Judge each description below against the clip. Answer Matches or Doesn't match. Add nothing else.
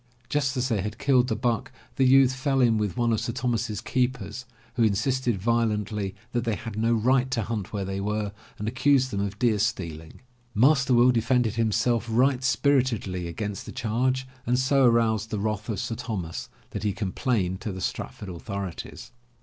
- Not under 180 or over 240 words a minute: Matches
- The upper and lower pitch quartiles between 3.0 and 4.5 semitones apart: Matches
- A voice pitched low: Matches